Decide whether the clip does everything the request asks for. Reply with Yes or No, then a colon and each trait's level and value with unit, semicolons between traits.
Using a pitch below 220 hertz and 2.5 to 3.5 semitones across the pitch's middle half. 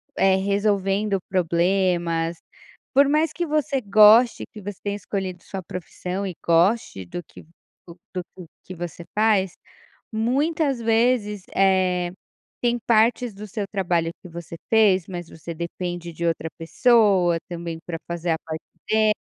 No: high, 190 Hz; average, 4.1 semitones